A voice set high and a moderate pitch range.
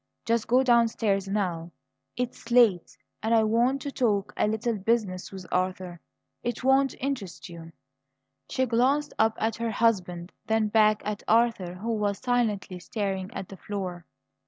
Yes: high, 215 Hz; average, 3.8 semitones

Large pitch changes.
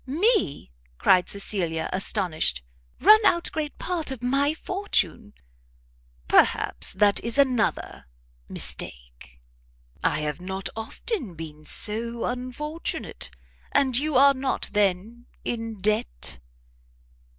Yes: wide, 7.2 semitones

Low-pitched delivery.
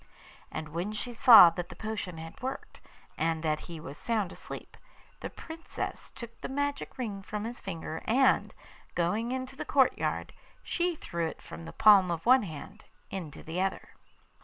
No: high, 200 Hz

